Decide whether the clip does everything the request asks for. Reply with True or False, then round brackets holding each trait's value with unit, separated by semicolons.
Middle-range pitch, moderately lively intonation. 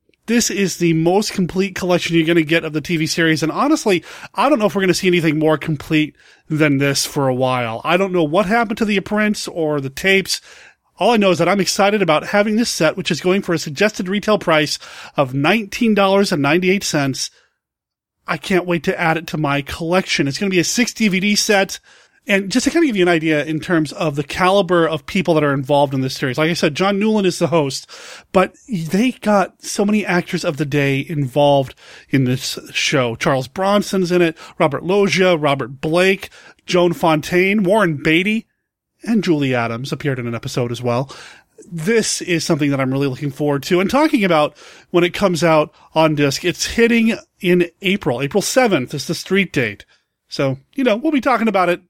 True (175 Hz; 4.5 semitones)